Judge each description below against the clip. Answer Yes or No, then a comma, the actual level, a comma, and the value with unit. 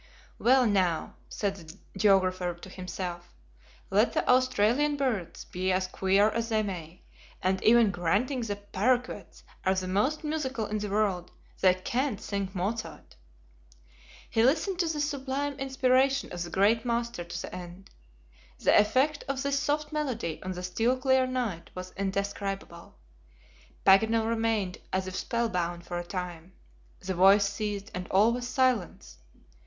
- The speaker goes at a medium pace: Yes, average, 150 wpm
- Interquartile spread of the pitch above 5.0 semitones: Yes, wide, 5.5 semitones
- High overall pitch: Yes, high, 205 Hz